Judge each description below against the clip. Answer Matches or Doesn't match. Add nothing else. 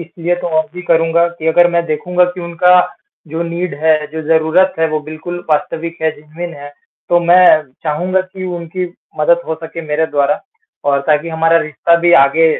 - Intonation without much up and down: Matches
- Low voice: Doesn't match